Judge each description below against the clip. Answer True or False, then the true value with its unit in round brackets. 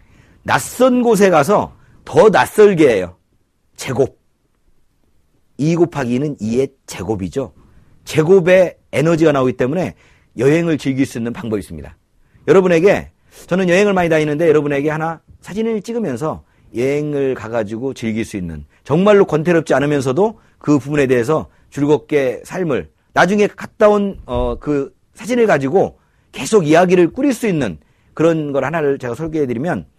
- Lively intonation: True (6.8 semitones)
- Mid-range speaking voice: True (150 Hz)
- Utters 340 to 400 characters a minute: False (310 characters per minute)